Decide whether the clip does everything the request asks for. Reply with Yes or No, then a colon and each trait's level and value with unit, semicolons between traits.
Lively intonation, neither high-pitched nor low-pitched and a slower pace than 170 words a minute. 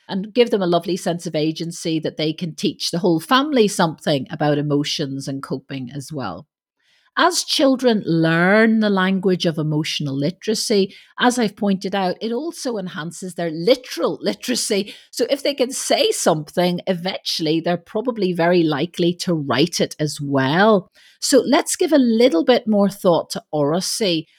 Yes: wide, 5.7 semitones; medium, 180 Hz; average, 160 wpm